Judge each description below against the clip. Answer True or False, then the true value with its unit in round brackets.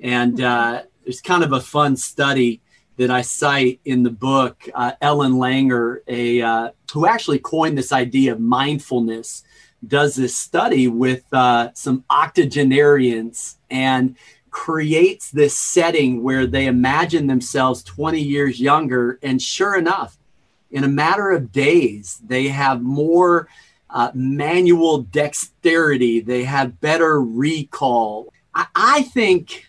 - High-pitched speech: False (135 Hz)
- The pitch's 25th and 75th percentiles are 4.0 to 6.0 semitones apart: False (3.1 semitones)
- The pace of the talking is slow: True (130 wpm)